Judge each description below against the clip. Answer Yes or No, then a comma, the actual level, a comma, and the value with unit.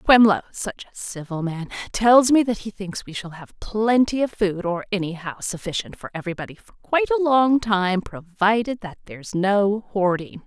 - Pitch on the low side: No, high, 200 Hz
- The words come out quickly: No, average, 170 wpm